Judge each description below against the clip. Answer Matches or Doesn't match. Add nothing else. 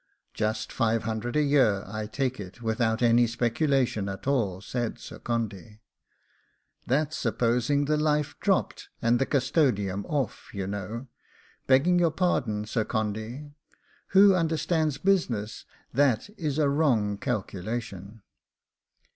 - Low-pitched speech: Matches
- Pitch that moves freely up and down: Doesn't match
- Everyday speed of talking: Doesn't match